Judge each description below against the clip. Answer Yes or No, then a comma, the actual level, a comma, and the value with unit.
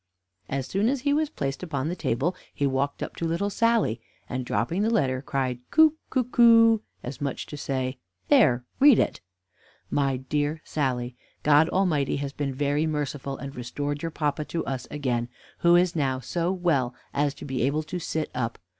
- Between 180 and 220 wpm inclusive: Yes, average, 190 wpm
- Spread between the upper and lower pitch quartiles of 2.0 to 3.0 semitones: No, average, 4.9 semitones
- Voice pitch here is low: No, medium, 145 Hz